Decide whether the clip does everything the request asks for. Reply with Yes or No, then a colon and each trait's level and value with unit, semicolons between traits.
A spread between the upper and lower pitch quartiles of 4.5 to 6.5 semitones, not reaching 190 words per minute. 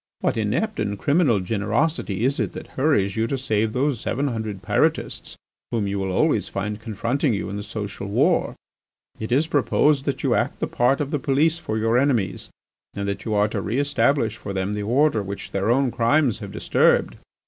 No: average, 5.2 semitones; average, 200 wpm